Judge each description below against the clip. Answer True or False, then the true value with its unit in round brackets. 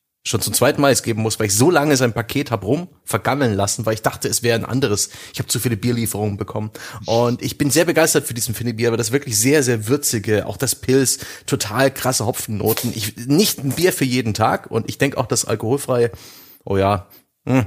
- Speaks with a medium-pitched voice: False (120 Hz)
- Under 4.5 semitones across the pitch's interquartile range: True (3.5 semitones)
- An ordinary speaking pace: False (225 wpm)